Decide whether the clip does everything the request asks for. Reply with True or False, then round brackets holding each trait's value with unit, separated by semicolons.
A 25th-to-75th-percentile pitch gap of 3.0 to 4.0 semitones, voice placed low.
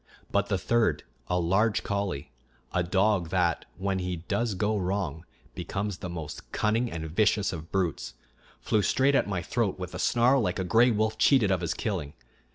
True (3.7 semitones; 95 Hz)